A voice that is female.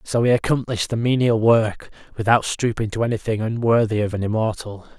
No: male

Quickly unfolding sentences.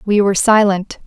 No: average, 170 wpm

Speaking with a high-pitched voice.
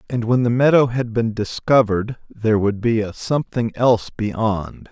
No: low, 115 Hz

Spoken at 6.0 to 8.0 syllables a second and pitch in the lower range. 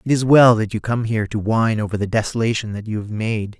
Yes: 6.3 syllables/s; low, 110 Hz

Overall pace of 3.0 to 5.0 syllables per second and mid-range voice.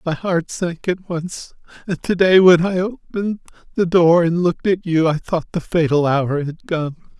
Yes: 4.6 syllables/s; medium, 170 Hz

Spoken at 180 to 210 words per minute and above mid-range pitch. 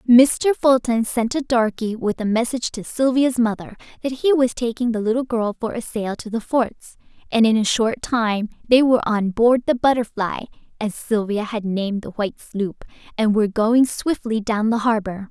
Yes: average, 190 wpm; high, 230 Hz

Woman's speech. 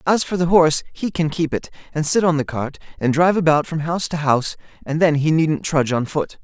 No: male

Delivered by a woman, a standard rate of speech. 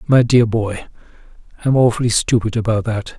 No: male; average, 150 wpm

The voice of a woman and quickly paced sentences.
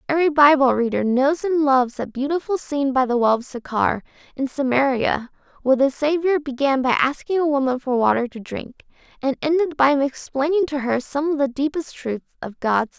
No: female; average, 195 wpm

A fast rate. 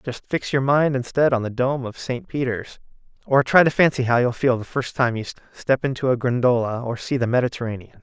Yes: fast, 225 wpm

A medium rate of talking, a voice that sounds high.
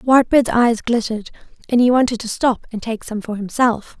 Yes: average, 195 wpm; high, 230 Hz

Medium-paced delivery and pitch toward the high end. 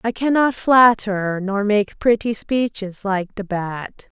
Yes: average, 145 wpm; high, 210 Hz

